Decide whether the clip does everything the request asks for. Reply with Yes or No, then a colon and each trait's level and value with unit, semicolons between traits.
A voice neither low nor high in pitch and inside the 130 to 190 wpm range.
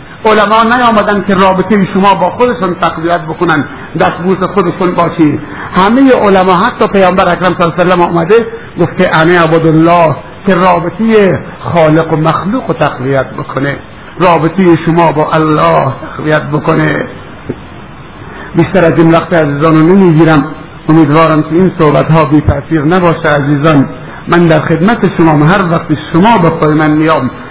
Yes: medium, 165 Hz; average, 150 wpm